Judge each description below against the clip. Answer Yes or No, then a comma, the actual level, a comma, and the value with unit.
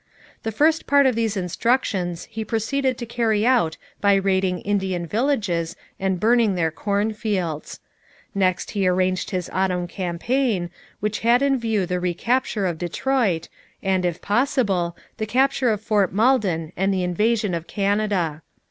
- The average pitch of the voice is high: Yes, high, 200 Hz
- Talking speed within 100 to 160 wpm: Yes, average, 150 wpm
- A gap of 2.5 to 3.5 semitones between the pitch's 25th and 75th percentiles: No, average, 4.4 semitones